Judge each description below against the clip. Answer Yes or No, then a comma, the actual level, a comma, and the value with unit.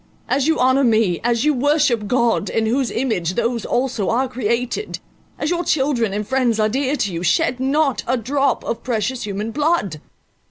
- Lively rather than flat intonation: No, average, 3.7 semitones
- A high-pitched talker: Yes, high, 245 Hz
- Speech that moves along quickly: No, average, 165 wpm